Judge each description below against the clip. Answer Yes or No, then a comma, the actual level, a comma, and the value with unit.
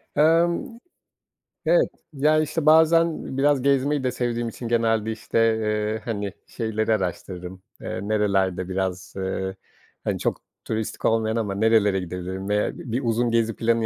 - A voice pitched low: Yes, low, 110 Hz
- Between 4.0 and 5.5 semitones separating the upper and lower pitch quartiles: Yes, average, 5.0 semitones